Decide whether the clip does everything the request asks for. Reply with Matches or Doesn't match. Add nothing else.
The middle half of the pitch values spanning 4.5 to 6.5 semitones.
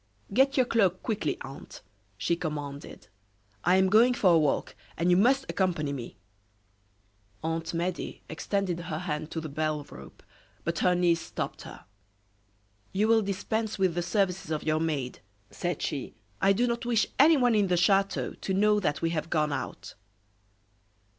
Matches